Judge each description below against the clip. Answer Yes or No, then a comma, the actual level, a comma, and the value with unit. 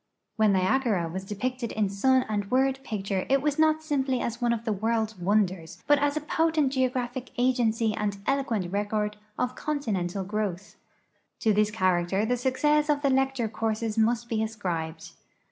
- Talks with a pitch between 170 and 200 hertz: No, high, 225 Hz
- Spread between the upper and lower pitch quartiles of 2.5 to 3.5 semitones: No, average, 4.4 semitones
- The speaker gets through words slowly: No, average, 165 wpm